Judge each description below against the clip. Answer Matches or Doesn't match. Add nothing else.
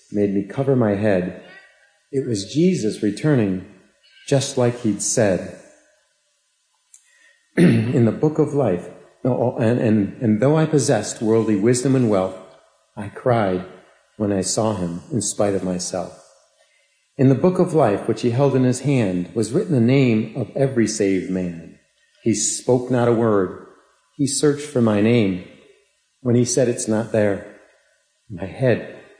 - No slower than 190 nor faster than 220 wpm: Doesn't match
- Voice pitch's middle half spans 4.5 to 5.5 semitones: Matches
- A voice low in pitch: Matches